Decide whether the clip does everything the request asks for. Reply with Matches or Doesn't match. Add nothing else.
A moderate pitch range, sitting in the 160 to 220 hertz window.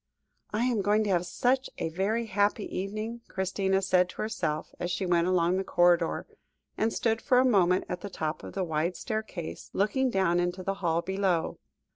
Matches